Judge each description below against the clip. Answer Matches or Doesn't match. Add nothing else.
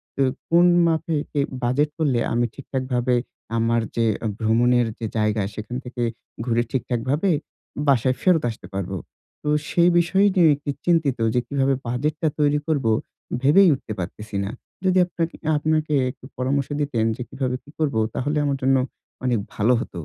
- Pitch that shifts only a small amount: Doesn't match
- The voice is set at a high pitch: Doesn't match